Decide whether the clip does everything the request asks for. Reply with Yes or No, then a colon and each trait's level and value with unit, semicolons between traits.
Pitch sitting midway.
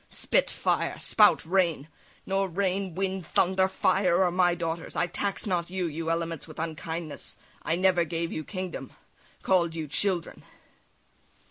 Yes: medium, 175 Hz